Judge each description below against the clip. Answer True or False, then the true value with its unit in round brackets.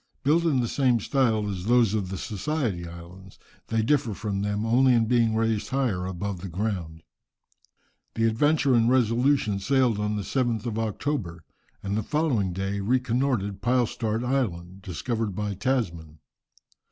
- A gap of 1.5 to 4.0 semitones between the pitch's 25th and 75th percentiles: False (4.4 semitones)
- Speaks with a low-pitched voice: True (110 Hz)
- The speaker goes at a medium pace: True (155 wpm)